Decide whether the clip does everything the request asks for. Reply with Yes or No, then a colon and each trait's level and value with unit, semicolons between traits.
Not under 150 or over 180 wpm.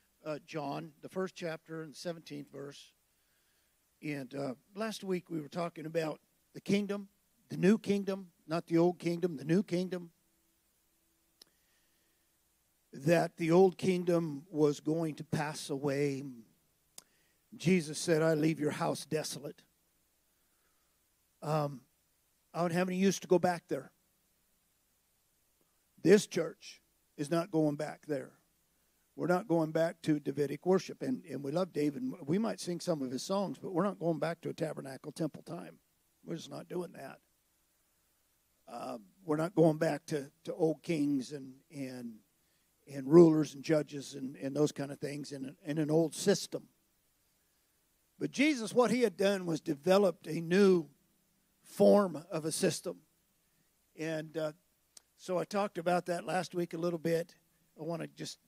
Yes: average, 155 wpm